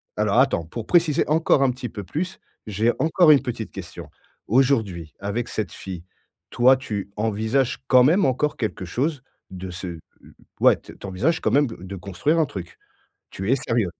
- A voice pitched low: Yes, low, 120 Hz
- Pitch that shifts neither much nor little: No, wide, 6.1 semitones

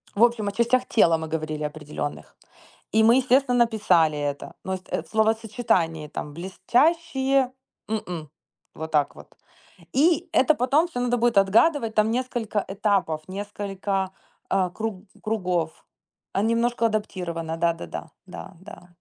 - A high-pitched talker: Yes, high, 205 Hz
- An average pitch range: No, wide, 5.9 semitones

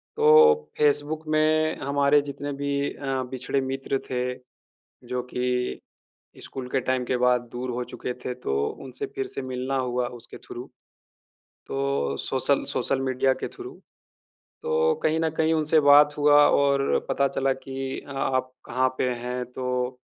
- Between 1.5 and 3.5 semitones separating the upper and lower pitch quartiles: Yes, narrow, 2.5 semitones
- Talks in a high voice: No, low, 135 Hz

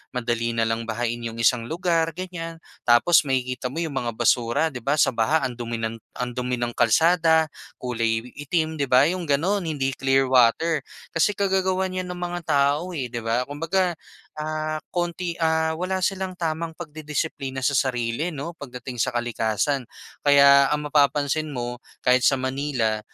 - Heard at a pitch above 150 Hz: No, medium, 140 Hz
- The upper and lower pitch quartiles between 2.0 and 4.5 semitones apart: No, average, 5.1 semitones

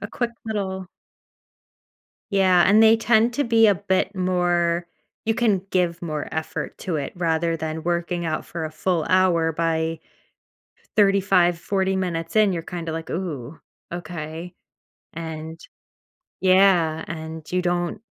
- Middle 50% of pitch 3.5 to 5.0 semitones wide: No, average, 2.7 semitones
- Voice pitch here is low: No, medium, 175 Hz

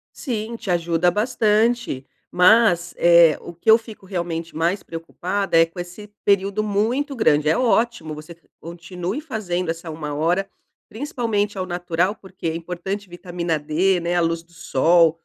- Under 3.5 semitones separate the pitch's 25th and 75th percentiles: No, average, 3.9 semitones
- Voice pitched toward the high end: No, medium, 180 Hz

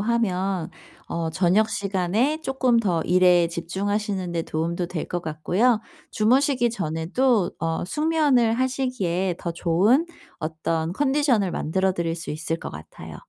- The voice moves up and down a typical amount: No, wide, 5.9 semitones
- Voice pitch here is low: No, high, 190 Hz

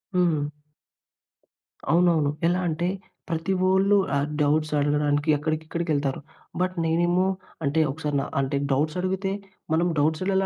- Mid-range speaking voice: Yes, medium, 160 Hz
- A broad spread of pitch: No, average, 3.4 semitones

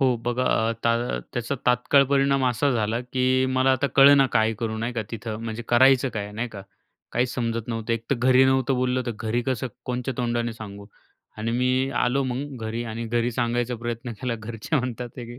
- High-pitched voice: No, low, 120 Hz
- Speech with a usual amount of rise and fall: No, narrow, 2.0 semitones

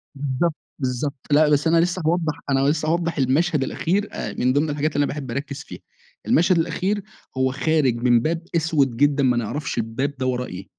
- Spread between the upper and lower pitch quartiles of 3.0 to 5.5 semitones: Yes, average, 3.8 semitones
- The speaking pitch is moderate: Yes, medium, 145 Hz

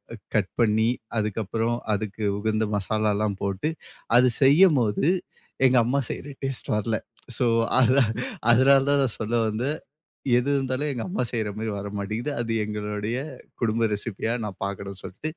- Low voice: Yes, low, 110 Hz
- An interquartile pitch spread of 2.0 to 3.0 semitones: No, average, 3.5 semitones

